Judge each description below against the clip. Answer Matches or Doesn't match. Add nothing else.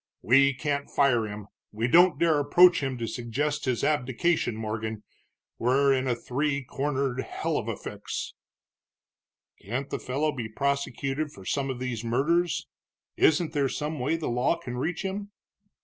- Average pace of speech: Matches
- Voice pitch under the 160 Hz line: Matches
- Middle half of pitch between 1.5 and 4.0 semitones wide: Matches